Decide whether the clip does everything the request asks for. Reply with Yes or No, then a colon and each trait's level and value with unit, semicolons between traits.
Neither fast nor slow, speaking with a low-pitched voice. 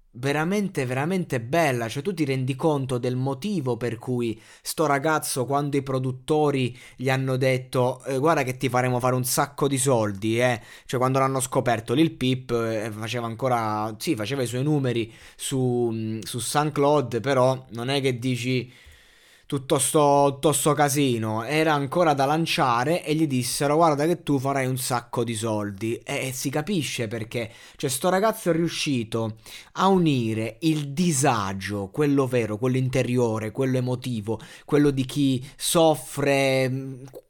Yes: average, 155 wpm; low, 130 Hz